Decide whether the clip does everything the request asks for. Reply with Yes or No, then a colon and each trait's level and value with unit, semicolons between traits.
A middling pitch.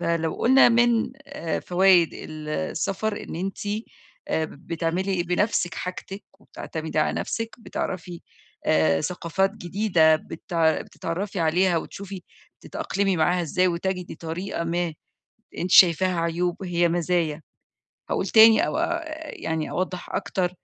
Yes: medium, 180 Hz